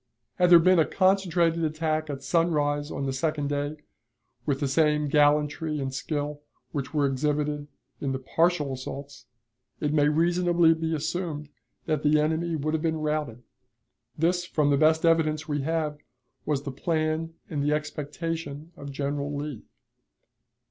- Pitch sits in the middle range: Yes, medium, 150 Hz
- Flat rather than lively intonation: Yes, narrow, 2.1 semitones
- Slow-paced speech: No, average, 155 wpm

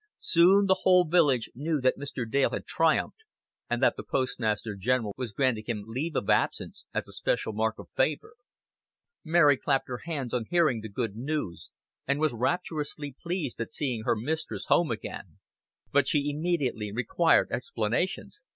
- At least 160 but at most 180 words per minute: Yes, average, 165 wpm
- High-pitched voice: No, low, 135 Hz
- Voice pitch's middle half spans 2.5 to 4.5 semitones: No, wide, 5.5 semitones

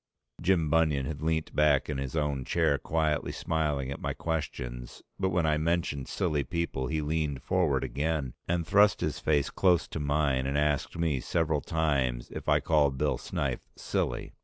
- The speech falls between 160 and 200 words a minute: Yes, average, 175 wpm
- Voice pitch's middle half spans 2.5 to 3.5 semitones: Yes, average, 2.8 semitones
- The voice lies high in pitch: No, very low, 75 Hz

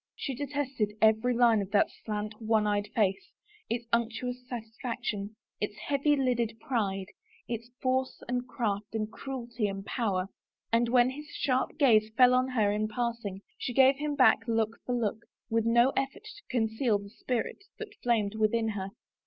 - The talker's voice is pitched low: No, high, 230 Hz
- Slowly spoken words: No, average, 165 wpm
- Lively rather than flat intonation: No, average, 3.0 semitones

